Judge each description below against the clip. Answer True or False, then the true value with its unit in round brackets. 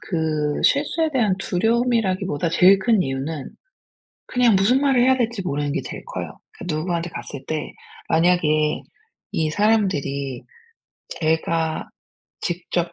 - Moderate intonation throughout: False (6.3 semitones)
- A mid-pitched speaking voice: True (175 Hz)